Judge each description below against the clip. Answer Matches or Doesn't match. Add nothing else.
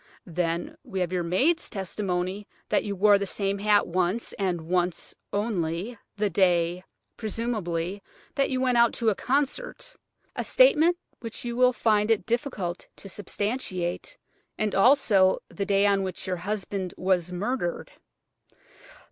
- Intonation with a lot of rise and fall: Doesn't match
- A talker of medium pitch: Doesn't match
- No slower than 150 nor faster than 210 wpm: Doesn't match